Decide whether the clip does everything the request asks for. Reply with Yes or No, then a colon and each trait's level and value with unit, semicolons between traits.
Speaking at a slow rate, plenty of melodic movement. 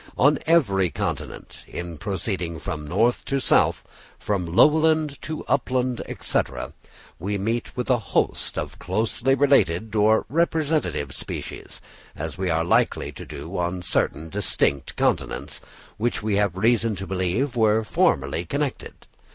Yes: slow, 130 wpm; wide, 6.5 semitones